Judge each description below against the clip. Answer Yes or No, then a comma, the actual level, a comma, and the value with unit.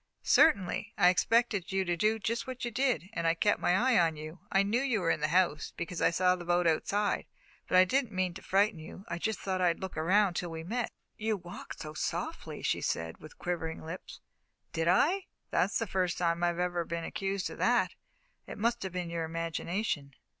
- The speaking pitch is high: No, medium, 180 Hz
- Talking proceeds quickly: Yes, fast, 220 wpm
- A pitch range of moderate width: Yes, average, 3.7 semitones